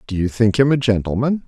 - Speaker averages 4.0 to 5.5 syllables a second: No, 6.0 syllables/s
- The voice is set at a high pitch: No, low, 115 Hz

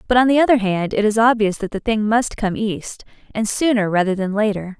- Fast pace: Yes, fast, 240 wpm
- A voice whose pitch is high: Yes, high, 215 Hz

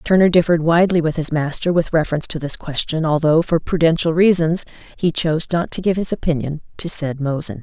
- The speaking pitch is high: No, medium, 165 Hz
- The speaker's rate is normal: Yes, average, 195 wpm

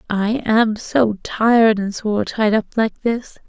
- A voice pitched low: No, high, 220 Hz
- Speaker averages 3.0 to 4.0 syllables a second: Yes, 3.5 syllables/s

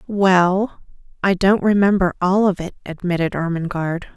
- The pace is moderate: No, slow, 130 wpm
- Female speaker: Yes, female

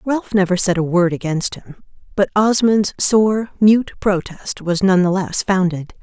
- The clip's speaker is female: Yes, female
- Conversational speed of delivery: Yes, average, 170 wpm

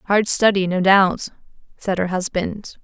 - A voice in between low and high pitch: No, high, 195 Hz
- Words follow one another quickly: No, average, 150 wpm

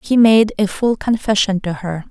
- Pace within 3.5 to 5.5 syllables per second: Yes, 4.7 syllables/s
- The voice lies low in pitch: No, high, 205 Hz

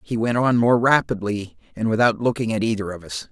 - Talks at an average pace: No, fast, 215 wpm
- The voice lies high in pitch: No, low, 110 Hz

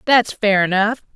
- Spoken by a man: No, female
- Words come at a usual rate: Yes, average, 155 wpm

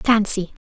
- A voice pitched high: Yes, high, 205 Hz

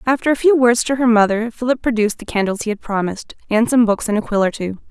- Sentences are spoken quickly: Yes, fast, 270 wpm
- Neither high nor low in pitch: No, high, 225 Hz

